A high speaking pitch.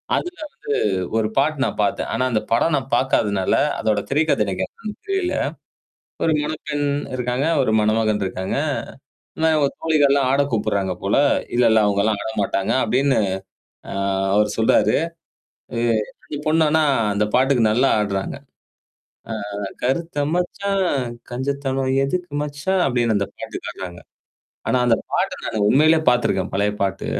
No: low, 130 Hz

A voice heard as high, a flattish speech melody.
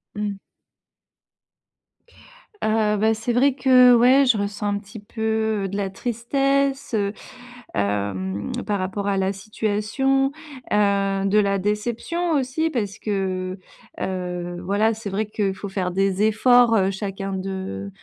No: high, 205 Hz; average, 3.2 semitones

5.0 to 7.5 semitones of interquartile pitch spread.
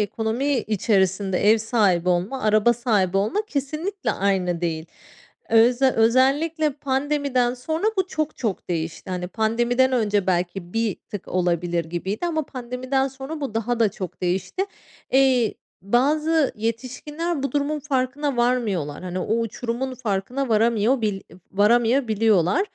Yes: wide, 5.4 semitones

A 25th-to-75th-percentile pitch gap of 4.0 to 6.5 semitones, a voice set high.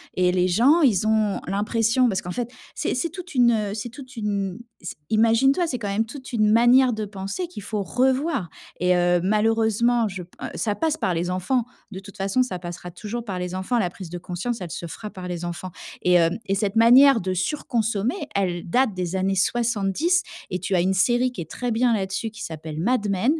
Yes: average, 4.8 semitones; high, 210 Hz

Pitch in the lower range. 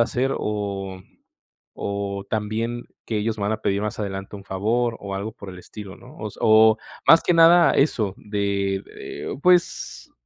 Yes: low, 105 Hz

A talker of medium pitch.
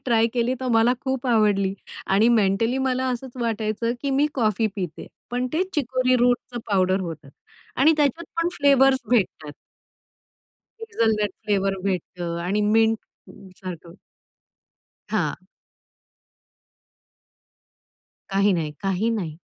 No: high, 225 Hz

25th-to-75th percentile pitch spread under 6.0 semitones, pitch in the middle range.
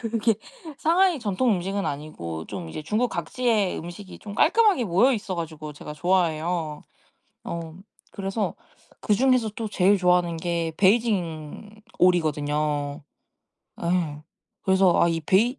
Yes: average, 5.3 semitones; medium, 180 Hz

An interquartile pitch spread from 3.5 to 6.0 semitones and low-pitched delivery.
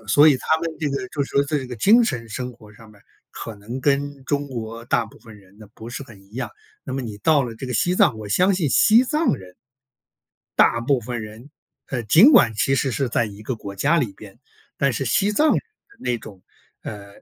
Yes: average, 4.9 semitones; low, 125 Hz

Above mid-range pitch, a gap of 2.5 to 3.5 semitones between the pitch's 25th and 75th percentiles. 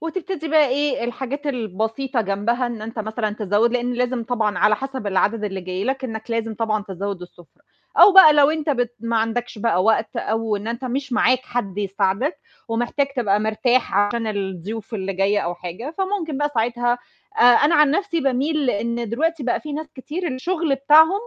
No: high, 240 Hz; average, 4.9 semitones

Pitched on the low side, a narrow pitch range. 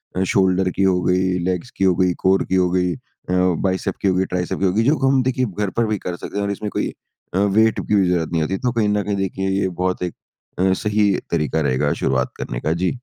Yes: very low, 95 Hz; narrow, 2.2 semitones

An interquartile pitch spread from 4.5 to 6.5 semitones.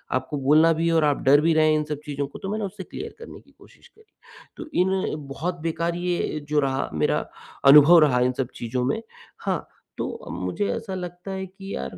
Yes: average, 4.8 semitones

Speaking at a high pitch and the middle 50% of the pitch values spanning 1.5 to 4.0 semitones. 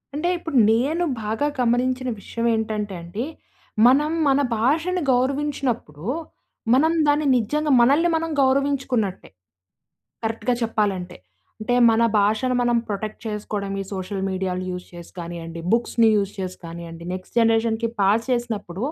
No: high, 225 Hz; average, 5.0 semitones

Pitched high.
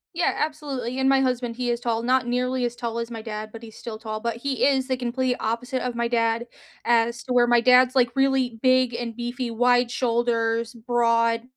Yes: high, 240 Hz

